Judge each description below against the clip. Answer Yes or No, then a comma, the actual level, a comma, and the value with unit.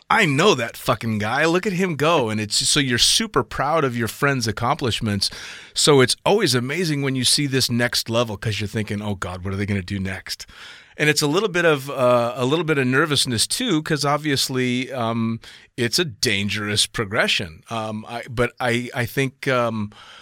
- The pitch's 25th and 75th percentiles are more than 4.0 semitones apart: Yes, average, 4.5 semitones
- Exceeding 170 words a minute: Yes, average, 200 wpm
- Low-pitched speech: Yes, low, 120 Hz